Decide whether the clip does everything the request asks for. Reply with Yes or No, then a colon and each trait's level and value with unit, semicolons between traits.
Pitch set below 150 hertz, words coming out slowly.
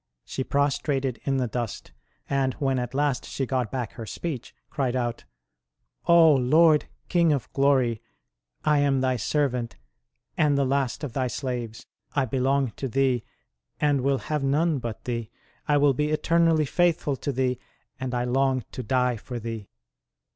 No: low, 135 Hz; average, 165 wpm